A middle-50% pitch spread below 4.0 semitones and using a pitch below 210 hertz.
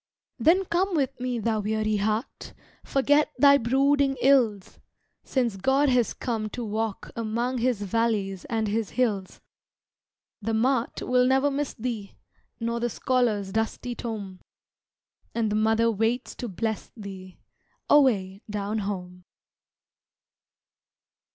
No: average, 3.4 semitones; high, 230 Hz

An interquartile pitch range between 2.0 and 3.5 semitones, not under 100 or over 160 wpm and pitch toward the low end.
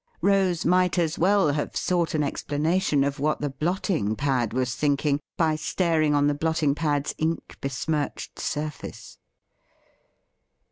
No: average, 2.8 semitones; slow, 135 wpm; medium, 150 Hz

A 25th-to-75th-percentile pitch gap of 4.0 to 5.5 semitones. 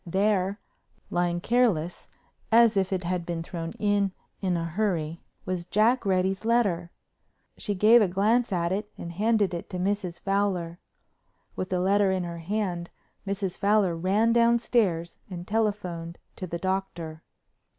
No: average, 3.3 semitones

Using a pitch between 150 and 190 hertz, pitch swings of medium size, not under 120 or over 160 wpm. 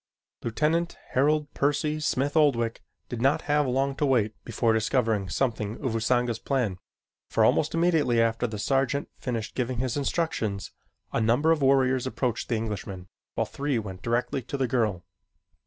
No: low, 125 Hz; average, 4.0 semitones; average, 155 wpm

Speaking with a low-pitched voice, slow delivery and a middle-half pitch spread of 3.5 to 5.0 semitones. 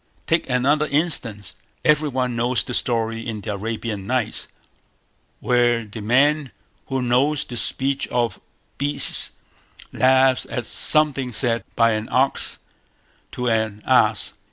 No: low, 125 Hz; slow, 130 wpm; average, 3.0 semitones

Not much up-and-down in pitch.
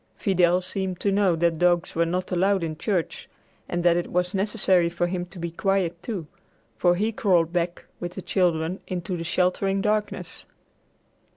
Yes: narrow, 2.0 semitones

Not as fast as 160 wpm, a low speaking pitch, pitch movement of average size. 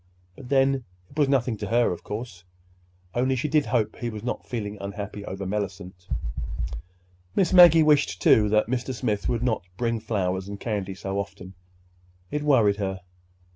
No: average, 165 wpm; low, 105 Hz; average, 4.6 semitones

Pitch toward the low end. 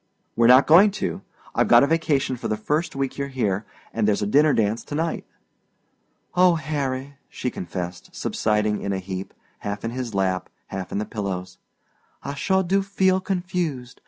Yes: low, 130 Hz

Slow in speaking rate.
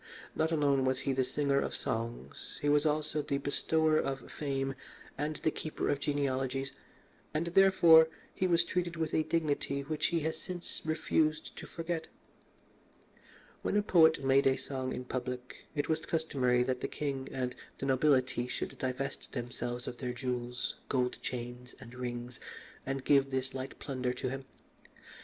No: average, 165 wpm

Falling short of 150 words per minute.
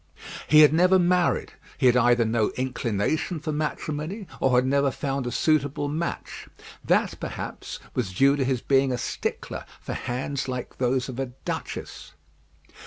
No: average, 160 wpm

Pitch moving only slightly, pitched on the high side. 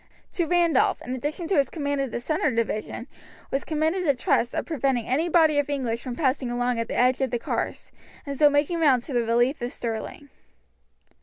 No: average, 4.0 semitones; very high, 275 Hz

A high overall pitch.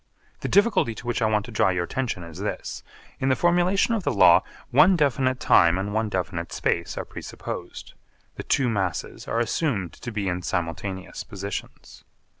No: low, 110 Hz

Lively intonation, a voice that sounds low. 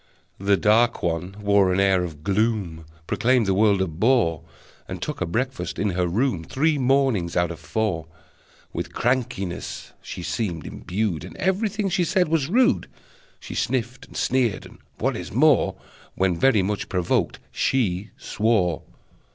Yes: wide, 6.5 semitones; low, 105 Hz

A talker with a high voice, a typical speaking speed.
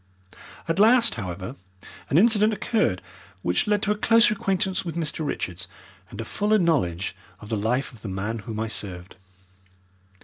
No: medium, 140 Hz; average, 165 wpm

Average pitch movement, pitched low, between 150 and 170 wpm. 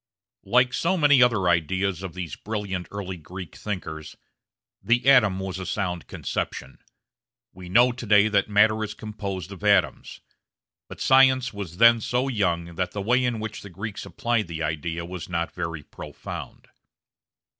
Yes: average, 4.5 semitones; low, 100 Hz; average, 160 wpm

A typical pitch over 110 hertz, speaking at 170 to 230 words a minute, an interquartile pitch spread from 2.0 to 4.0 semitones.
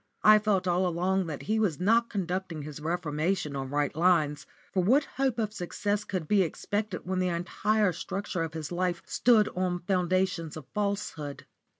Yes: medium, 185 Hz; average, 175 wpm; average, 3.7 semitones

